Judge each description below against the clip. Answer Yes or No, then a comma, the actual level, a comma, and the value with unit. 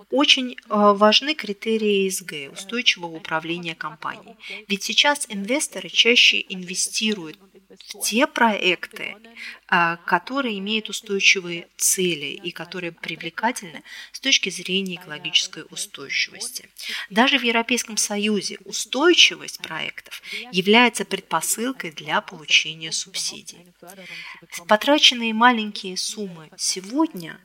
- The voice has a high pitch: Yes, high, 200 Hz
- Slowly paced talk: Yes, slow, 90 wpm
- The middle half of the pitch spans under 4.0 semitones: No, average, 4.4 semitones